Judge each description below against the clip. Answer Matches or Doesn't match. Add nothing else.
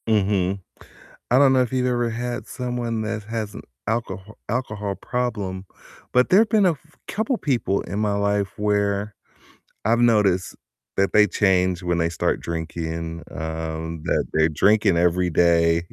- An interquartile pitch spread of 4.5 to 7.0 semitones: Matches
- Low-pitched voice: Matches